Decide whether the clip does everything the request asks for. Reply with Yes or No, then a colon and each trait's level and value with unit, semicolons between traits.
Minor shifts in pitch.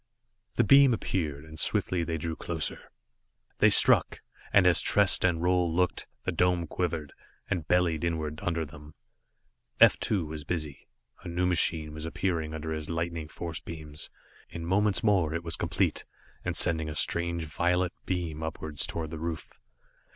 Yes: narrow, 2.2 semitones